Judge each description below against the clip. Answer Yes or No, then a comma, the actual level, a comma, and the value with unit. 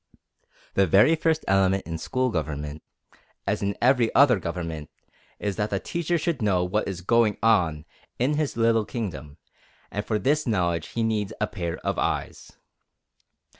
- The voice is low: Yes, low, 105 Hz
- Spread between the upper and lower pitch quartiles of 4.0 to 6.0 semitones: Yes, average, 5.0 semitones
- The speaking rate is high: No, average, 160 wpm